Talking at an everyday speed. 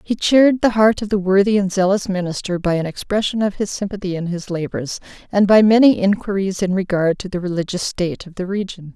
No: fast, 215 wpm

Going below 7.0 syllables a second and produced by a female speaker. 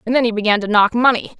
No: 7.4 syllables/s; female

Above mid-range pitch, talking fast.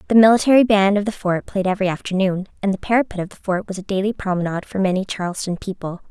Yes: high, 195 Hz; fast, 225 wpm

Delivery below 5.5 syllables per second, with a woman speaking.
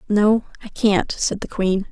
Yes: 4.0 syllables/s; female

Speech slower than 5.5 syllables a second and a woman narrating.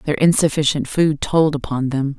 Yes: 4.7 syllables/s; female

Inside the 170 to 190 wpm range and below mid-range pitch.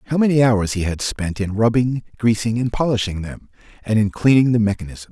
No: average, 200 wpm; low, 110 Hz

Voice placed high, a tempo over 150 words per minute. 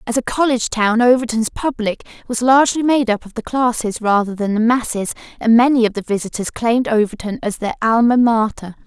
Yes: high, 230 Hz; average, 190 wpm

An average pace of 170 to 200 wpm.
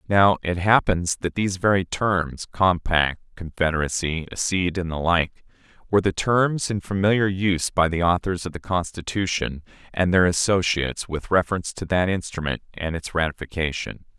No: average, 145 wpm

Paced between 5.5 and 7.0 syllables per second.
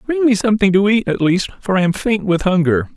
Yes: 5.9 syllables/s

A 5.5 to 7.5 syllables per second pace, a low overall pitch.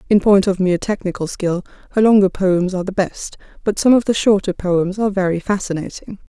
No: 5.9 syllables/s; high, 190 Hz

